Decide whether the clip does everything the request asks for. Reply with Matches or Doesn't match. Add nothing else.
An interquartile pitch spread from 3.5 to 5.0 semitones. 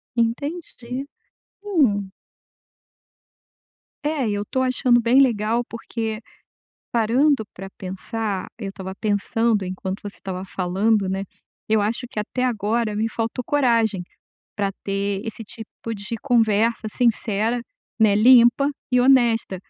Doesn't match